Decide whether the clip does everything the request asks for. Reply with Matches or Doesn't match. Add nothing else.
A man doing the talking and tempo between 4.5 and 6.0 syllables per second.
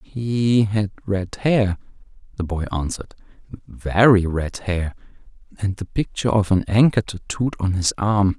Doesn't match